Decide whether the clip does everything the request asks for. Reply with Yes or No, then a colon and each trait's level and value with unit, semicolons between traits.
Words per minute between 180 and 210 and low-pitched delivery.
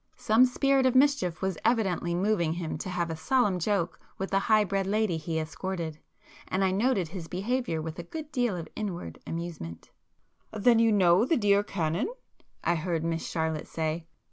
No: average, 185 wpm; medium, 185 Hz